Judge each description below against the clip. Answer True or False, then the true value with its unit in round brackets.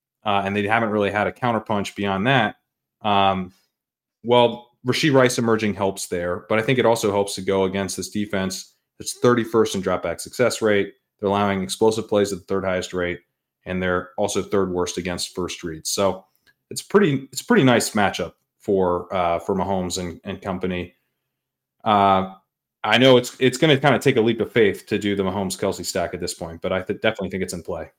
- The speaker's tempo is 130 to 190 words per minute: False (205 wpm)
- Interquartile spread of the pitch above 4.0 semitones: False (3.2 semitones)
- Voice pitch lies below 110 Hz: True (100 Hz)